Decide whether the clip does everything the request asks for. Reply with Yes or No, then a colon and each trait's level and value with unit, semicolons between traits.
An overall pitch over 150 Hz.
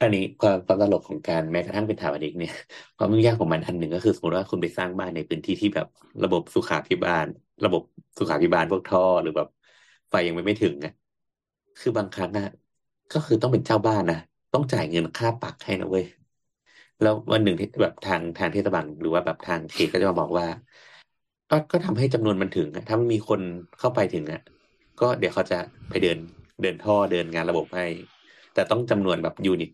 No: low, 100 Hz